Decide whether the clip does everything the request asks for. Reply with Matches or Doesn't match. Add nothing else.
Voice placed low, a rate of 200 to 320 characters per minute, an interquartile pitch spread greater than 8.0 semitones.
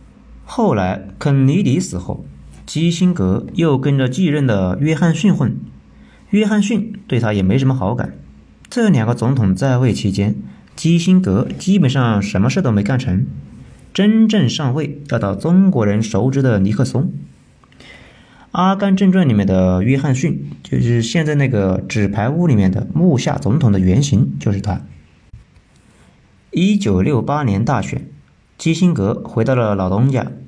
Matches